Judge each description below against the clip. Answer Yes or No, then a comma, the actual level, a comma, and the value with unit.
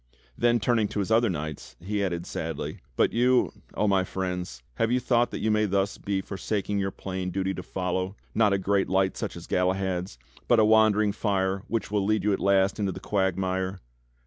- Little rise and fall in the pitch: Yes, narrow, 2.3 semitones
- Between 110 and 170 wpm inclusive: No, average, 200 wpm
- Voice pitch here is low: Yes, low, 100 Hz